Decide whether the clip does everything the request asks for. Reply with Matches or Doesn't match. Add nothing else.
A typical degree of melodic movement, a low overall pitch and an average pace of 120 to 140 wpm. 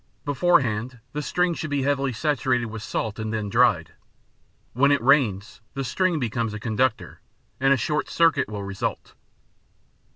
Doesn't match